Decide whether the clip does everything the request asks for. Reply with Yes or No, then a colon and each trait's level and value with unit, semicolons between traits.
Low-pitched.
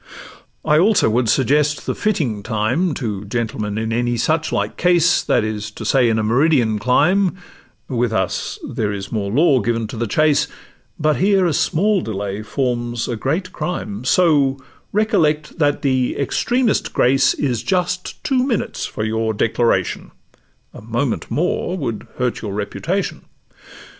Yes: low, 130 Hz